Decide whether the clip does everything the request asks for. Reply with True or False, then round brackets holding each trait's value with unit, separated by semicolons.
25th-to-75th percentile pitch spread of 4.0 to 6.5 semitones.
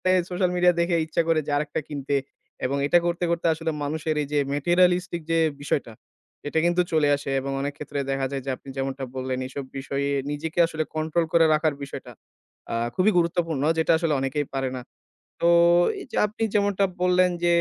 False (3.6 semitones)